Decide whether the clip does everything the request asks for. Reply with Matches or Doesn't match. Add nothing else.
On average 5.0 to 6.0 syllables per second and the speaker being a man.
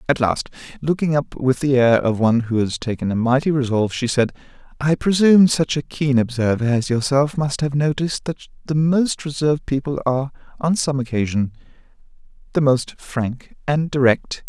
Matches